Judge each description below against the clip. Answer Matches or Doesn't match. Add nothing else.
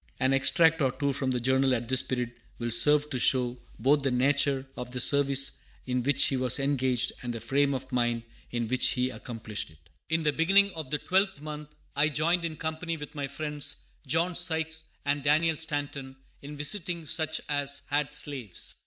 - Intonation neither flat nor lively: Matches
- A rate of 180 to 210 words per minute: Matches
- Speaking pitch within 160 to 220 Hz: Doesn't match